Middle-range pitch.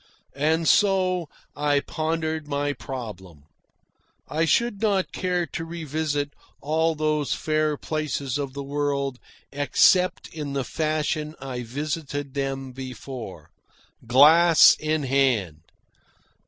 Yes: medium, 145 Hz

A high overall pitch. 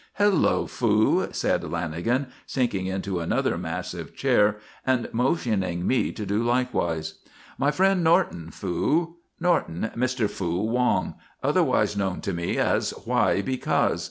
No: low, 110 Hz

